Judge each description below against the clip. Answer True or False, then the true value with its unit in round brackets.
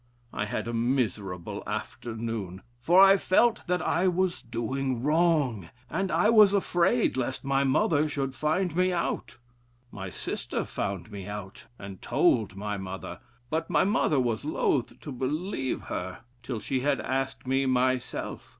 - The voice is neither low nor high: False (130 Hz)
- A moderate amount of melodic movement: False (6.9 semitones)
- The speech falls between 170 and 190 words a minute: False (150 wpm)